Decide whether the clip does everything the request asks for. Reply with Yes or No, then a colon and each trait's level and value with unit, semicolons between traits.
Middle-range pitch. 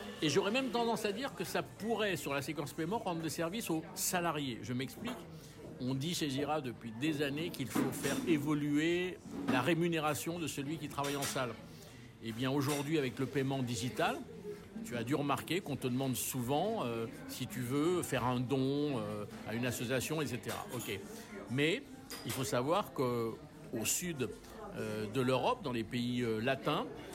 Yes: medium, 145 Hz